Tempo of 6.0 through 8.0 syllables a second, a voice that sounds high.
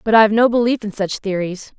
Yes: 6.1 syllables/s; high, 210 Hz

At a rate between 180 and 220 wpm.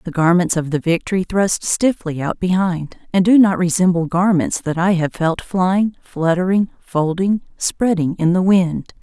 No: average, 165 wpm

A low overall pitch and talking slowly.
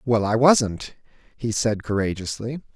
Yes: low, 115 Hz; slow, 130 wpm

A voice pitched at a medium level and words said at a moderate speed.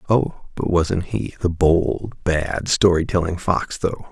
No: very low, 90 Hz; average, 160 wpm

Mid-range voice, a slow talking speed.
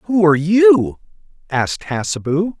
Yes: medium, 165 Hz; slow, 115 wpm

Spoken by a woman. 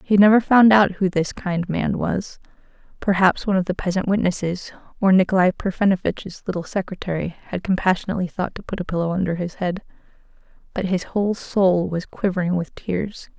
Yes: female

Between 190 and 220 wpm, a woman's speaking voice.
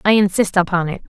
Yes: fast, 205 wpm; female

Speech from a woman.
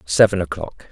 No: male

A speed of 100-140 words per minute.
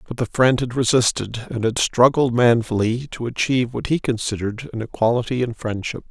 No: average, 175 wpm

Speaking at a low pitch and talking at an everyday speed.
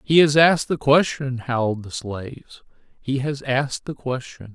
Yes: low, 130 Hz; average, 160 wpm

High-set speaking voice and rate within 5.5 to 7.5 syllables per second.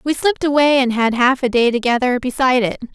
Yes: very high, 255 Hz; 6.3 syllables/s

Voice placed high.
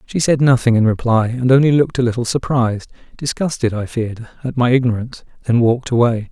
No: low, 120 Hz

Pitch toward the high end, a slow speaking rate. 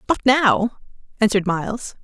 Yes: high, 225 Hz; slow, 120 wpm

